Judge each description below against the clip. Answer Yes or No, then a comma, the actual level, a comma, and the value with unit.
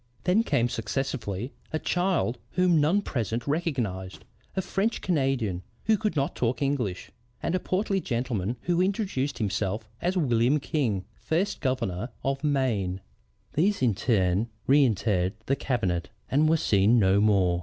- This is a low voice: Yes, low, 130 Hz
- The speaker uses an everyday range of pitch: No, wide, 7.4 semitones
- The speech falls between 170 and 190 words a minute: No, average, 145 wpm